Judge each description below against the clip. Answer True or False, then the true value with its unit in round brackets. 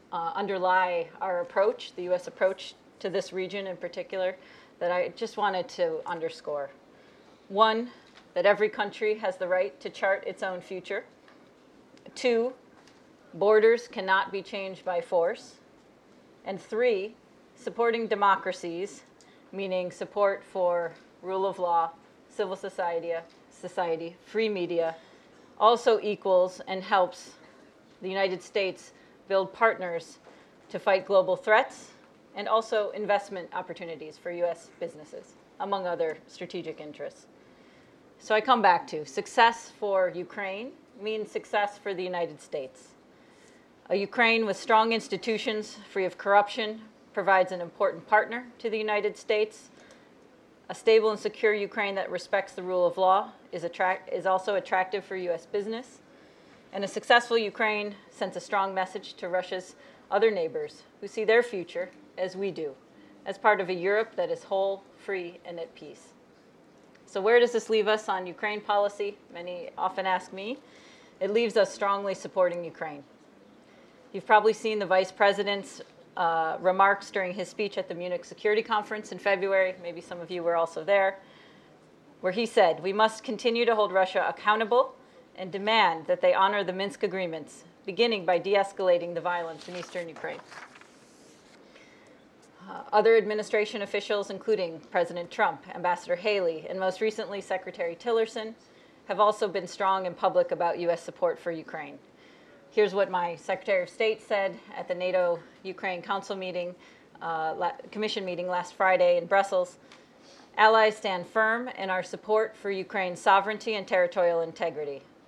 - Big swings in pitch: False (3.1 semitones)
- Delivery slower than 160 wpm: True (150 wpm)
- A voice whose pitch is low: False (195 Hz)